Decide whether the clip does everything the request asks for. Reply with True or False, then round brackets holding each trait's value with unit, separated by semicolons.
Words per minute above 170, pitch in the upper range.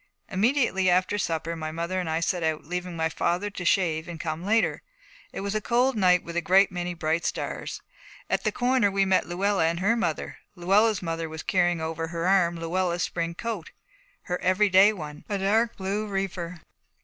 False (190 wpm; 180 Hz)